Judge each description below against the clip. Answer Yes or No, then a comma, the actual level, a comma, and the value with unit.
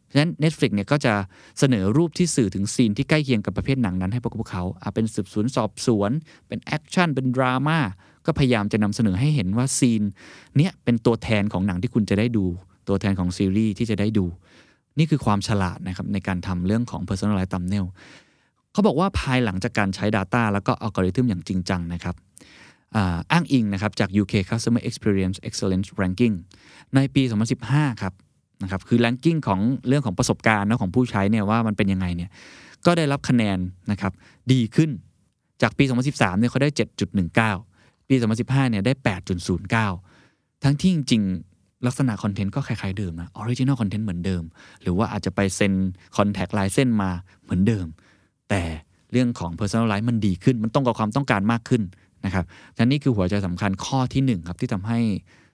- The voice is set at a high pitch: No, low, 110 Hz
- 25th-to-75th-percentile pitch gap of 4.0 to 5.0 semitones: Yes, average, 4.6 semitones